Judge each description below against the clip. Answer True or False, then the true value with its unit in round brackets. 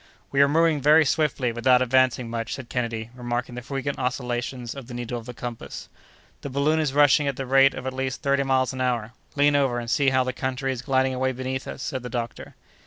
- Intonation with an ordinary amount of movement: False (2.1 semitones)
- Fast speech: True (230 wpm)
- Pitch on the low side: True (130 Hz)